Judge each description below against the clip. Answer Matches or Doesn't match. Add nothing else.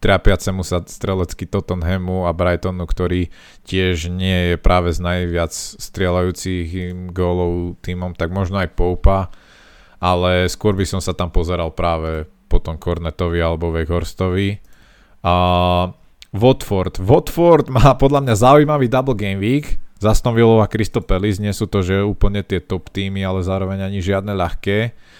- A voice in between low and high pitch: Doesn't match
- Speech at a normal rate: Matches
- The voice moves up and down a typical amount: Doesn't match